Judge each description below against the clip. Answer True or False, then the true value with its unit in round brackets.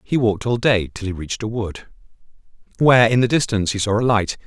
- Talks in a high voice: False (110 Hz)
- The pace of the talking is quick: True (230 wpm)